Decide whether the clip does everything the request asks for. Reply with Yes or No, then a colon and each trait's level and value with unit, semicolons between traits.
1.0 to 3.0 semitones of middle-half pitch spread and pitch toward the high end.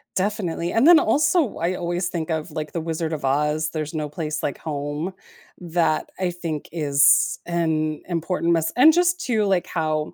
No: average, 2.7 semitones; medium, 165 Hz